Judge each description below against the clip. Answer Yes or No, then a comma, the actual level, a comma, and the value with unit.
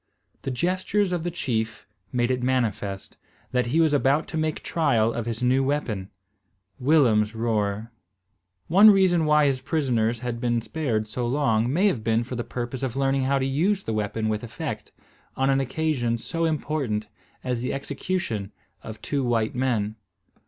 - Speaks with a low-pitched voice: Yes, low, 125 Hz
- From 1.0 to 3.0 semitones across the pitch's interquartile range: No, average, 4.9 semitones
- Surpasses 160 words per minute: Yes, average, 170 wpm